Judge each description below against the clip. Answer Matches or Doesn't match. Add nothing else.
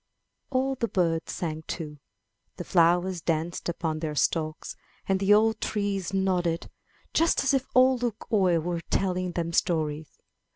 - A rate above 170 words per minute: Doesn't match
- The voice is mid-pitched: Matches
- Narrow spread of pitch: Doesn't match